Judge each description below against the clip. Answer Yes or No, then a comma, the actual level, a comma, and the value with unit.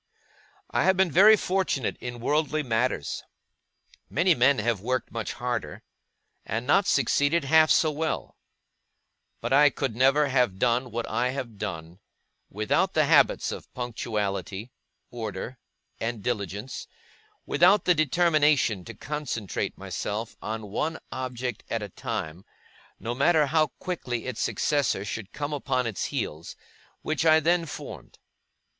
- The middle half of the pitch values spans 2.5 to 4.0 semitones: No, average, 5.3 semitones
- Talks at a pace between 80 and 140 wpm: Yes, slow, 135 wpm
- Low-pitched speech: Yes, low, 125 Hz